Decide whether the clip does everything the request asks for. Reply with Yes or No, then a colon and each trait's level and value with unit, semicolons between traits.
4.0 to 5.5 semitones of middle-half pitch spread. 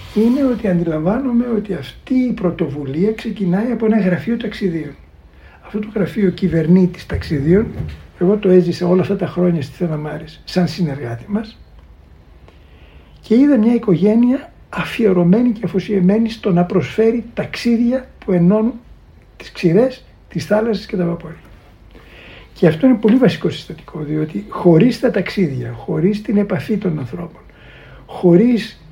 Yes: average, 5.2 semitones